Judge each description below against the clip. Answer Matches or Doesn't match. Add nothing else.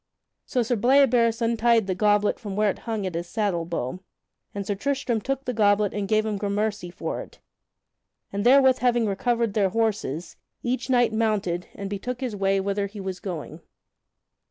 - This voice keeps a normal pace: Matches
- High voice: Matches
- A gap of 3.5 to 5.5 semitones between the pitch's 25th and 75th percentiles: Doesn't match